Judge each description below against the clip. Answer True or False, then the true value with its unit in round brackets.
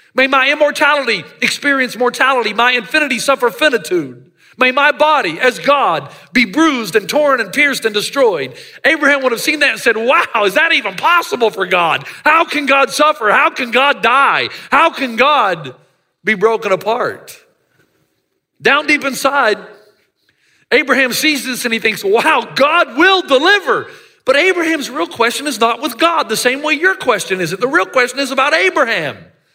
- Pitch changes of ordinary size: True (4.8 semitones)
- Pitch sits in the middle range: False (275 Hz)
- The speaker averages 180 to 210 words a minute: False (170 wpm)